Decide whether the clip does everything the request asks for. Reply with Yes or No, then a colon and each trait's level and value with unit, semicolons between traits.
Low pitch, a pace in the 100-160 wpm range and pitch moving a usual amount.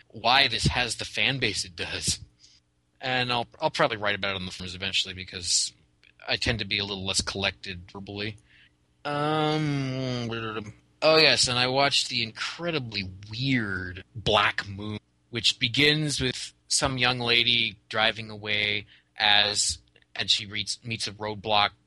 Yes: low, 105 Hz; average, 150 wpm; average, 4.1 semitones